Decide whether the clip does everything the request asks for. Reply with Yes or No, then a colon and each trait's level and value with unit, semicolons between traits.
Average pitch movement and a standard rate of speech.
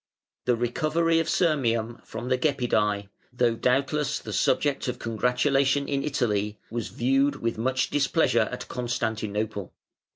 No: average, 3.6 semitones; slow, 130 wpm